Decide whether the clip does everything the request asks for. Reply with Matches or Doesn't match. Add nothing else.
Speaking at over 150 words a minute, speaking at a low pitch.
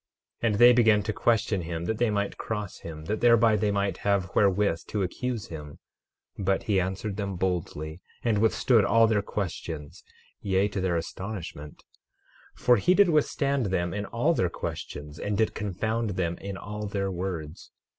Matches